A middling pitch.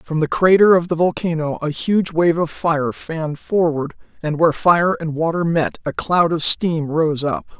Yes: medium, 165 Hz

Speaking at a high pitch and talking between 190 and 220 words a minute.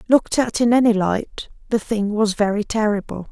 No: high, 215 Hz; average, 180 wpm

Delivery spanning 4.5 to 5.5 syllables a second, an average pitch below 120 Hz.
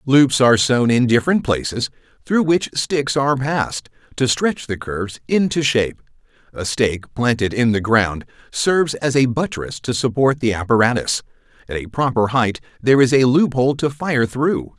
No: 5.0 syllables/s; low, 125 Hz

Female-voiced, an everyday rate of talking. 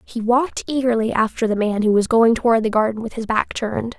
No: female; fast, 240 wpm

